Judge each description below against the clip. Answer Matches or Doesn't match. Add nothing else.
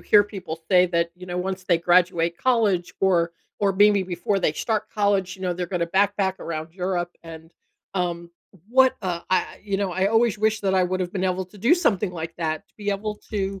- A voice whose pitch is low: Doesn't match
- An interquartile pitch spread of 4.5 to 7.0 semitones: Doesn't match